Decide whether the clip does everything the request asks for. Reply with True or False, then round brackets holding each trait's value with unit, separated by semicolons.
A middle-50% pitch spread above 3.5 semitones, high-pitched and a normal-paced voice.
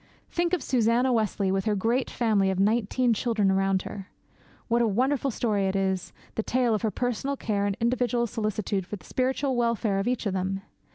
True (3.9 semitones; 220 Hz; 195 wpm)